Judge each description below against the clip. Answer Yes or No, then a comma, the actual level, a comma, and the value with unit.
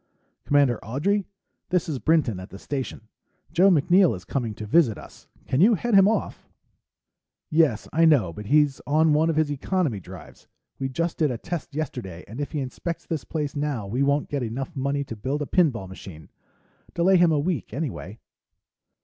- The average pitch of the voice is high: No, medium, 145 Hz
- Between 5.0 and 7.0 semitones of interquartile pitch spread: Yes, wide, 5.5 semitones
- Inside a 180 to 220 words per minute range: Yes, average, 185 wpm